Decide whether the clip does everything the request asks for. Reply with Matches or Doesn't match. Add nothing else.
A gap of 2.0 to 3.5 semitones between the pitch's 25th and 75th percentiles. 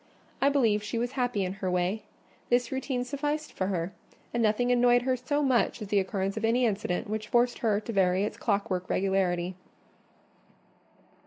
Doesn't match